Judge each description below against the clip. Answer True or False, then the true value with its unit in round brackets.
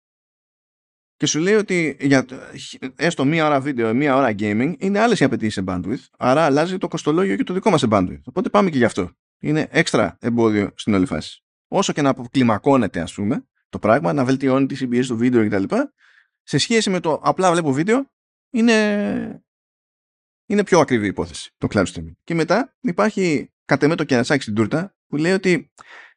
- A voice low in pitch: False (145 Hz)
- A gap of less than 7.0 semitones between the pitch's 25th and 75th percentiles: False (7.3 semitones)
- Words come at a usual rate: False (190 wpm)